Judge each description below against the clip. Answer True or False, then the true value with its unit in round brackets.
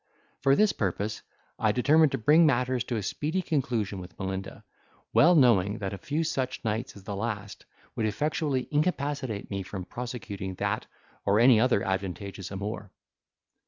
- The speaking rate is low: False (160 wpm)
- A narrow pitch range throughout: False (5.6 semitones)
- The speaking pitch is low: True (115 Hz)